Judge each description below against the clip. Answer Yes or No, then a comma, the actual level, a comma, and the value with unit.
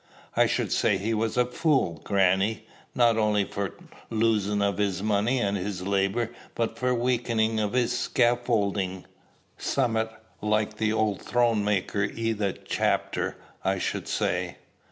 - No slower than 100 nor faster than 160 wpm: Yes, average, 145 wpm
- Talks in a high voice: No, low, 110 Hz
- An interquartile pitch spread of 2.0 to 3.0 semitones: Yes, average, 2.7 semitones